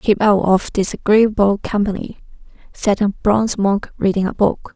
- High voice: Yes, high, 200 Hz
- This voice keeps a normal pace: Yes, average, 150 wpm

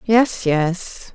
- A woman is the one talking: Yes, female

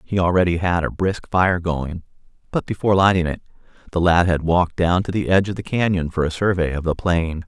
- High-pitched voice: No, very low, 90 Hz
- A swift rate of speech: Yes, fast, 225 wpm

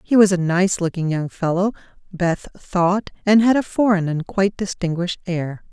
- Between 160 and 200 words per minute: Yes, average, 180 wpm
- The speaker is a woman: Yes, female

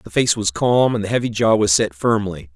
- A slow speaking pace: No, fast, 260 wpm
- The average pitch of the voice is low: Yes, low, 105 Hz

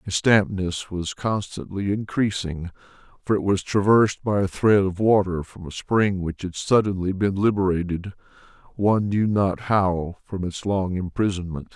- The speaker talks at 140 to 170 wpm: Yes, average, 155 wpm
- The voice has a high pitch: No, very low, 95 Hz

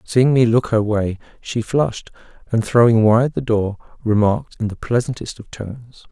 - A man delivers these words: Yes, male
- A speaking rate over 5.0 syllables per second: No, 4.9 syllables/s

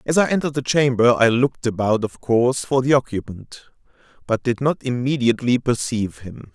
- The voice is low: Yes, low, 125 Hz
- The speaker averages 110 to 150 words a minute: No, average, 175 wpm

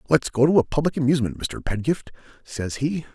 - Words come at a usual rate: Yes, average, 190 wpm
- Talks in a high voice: No, low, 135 Hz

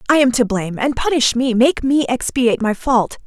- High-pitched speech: Yes, high, 245 Hz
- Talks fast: Yes, fast, 220 wpm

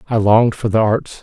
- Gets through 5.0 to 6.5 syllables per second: Yes, 5.8 syllables/s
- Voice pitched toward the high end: No, low, 110 Hz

